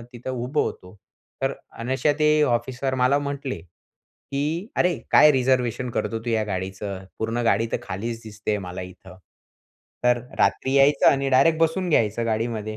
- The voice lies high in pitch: No, low, 120 Hz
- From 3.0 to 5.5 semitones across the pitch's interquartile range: Yes, average, 4.2 semitones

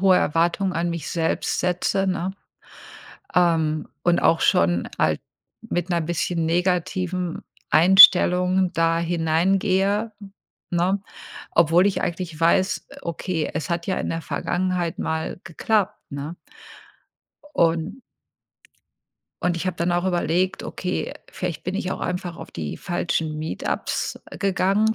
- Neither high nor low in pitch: Yes, medium, 175 Hz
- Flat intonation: Yes, narrow, 2.1 semitones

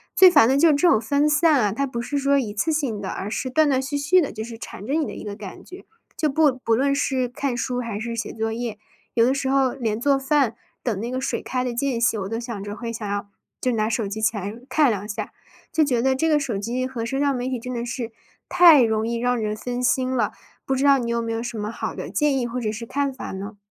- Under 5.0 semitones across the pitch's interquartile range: Yes, average, 3.7 semitones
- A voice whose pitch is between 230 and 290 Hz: Yes, high, 245 Hz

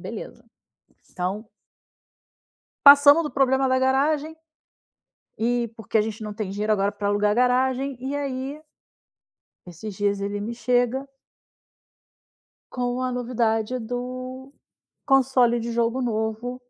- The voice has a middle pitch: No, high, 245 Hz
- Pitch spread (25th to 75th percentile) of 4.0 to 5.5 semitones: No, average, 3.3 semitones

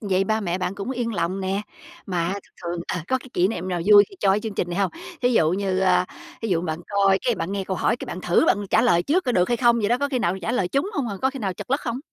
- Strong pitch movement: No, average, 4.7 semitones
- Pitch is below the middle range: No, high, 200 Hz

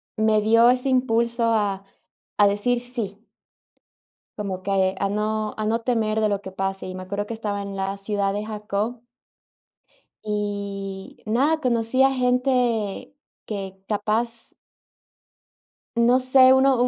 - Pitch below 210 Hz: No, high, 215 Hz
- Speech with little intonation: No, average, 3.1 semitones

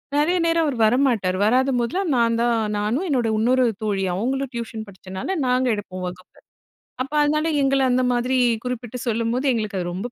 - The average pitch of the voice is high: Yes, high, 240 Hz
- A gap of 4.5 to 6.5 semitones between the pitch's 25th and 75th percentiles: No, average, 3.8 semitones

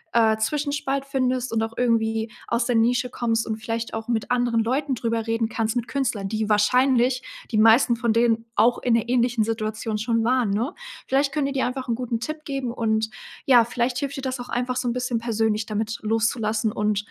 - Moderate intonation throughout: No, narrow, 2.1 semitones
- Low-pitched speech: No, high, 235 Hz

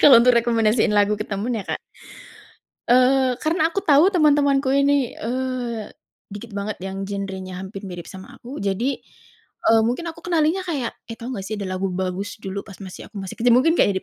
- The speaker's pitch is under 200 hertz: No, high, 230 Hz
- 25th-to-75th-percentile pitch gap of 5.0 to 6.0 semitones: Yes, wide, 5.5 semitones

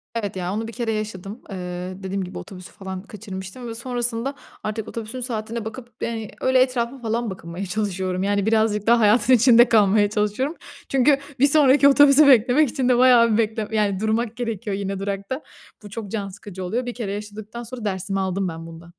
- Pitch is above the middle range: Yes, high, 220 Hz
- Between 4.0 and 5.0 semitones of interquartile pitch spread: No, average, 3.5 semitones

